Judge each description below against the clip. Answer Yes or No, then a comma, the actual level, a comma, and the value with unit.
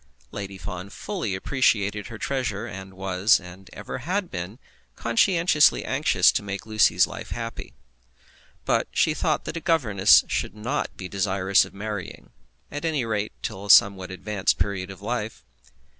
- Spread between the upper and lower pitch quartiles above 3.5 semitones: Yes, average, 4.0 semitones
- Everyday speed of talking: Yes, average, 155 wpm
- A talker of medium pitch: No, low, 105 Hz